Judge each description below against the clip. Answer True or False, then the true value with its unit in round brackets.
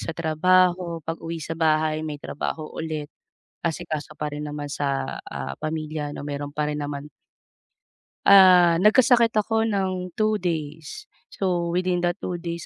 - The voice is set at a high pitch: False (165 Hz)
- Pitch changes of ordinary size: True (3.4 semitones)